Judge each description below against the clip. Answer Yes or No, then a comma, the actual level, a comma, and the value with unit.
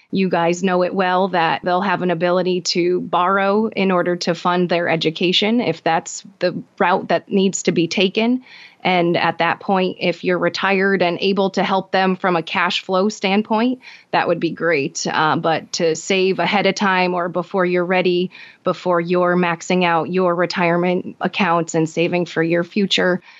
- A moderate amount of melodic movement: No, narrow, 1.8 semitones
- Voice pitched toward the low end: No, medium, 180 Hz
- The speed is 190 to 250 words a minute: No, average, 180 wpm